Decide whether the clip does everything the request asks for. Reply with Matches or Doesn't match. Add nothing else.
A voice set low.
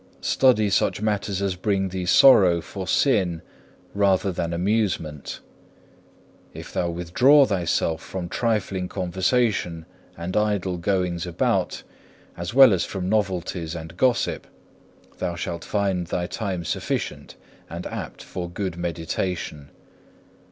Matches